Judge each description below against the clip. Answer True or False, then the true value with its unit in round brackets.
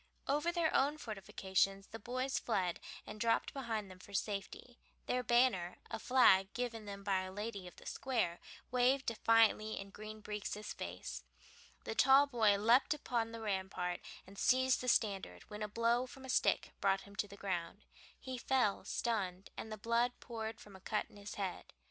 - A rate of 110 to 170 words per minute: False (180 wpm)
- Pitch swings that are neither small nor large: True (3.9 semitones)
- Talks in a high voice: True (215 Hz)